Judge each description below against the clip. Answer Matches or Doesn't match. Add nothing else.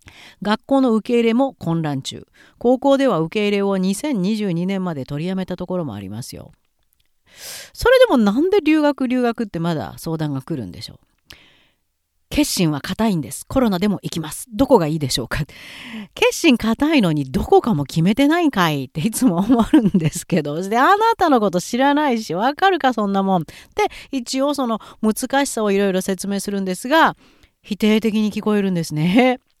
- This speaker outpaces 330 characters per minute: Matches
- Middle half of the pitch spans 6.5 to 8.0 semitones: Matches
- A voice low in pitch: Doesn't match